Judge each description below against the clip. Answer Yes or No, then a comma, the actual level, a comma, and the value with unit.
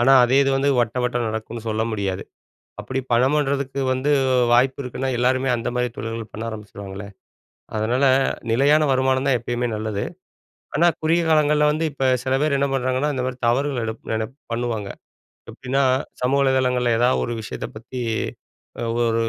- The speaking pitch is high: No, low, 125 Hz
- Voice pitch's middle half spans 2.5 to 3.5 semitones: Yes, average, 3.0 semitones